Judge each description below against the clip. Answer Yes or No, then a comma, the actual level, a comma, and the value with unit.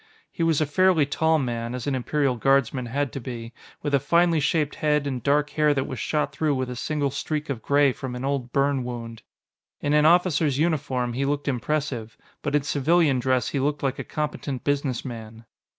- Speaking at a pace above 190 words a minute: Yes, average, 200 wpm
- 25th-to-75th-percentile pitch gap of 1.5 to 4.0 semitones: Yes, average, 3.0 semitones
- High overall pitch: No, medium, 140 Hz